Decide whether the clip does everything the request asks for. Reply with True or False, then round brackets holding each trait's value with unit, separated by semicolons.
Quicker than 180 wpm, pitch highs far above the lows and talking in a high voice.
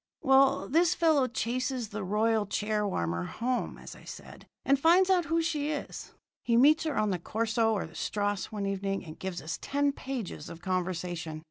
True (190 wpm; 6.4 semitones; 225 Hz)